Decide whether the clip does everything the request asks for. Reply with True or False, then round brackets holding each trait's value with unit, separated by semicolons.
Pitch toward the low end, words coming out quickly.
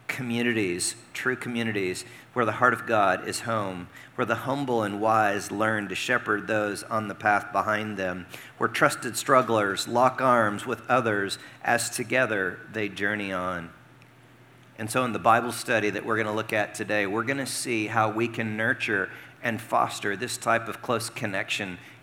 False (110 Hz; 175 wpm)